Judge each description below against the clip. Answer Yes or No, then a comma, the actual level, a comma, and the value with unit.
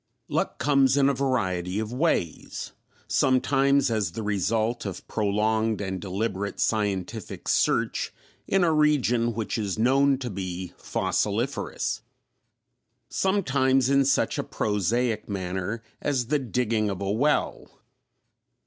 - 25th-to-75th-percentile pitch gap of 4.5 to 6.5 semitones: Yes, average, 5.0 semitones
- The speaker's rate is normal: No, slow, 125 wpm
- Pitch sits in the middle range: No, low, 115 Hz